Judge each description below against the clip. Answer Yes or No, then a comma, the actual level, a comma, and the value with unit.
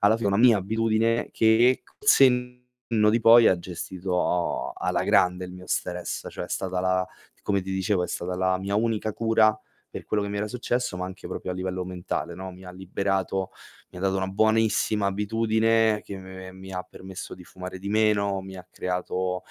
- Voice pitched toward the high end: No, very low, 95 Hz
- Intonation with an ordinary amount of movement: Yes, average, 3.0 semitones